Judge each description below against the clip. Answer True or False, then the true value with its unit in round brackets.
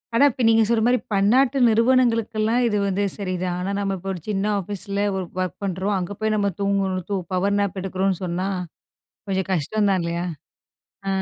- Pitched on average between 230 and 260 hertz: False (200 Hz)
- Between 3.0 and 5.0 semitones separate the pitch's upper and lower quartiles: False (2.6 semitones)